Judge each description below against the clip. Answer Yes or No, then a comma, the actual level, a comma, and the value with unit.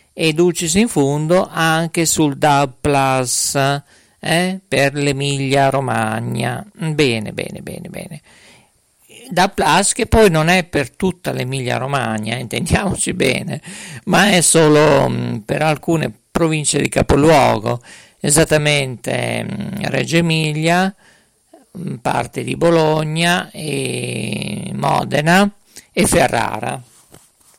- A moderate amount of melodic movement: Yes, average, 4.1 semitones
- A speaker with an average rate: No, slow, 105 wpm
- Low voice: No, medium, 155 Hz